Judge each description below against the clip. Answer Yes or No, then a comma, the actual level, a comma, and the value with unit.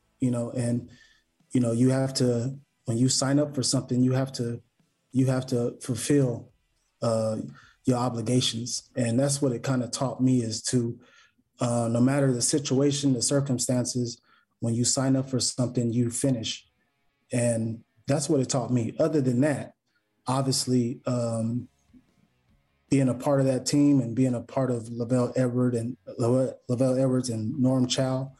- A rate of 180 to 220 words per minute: No, average, 165 wpm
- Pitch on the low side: Yes, low, 125 Hz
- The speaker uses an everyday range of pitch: No, narrow, 1.8 semitones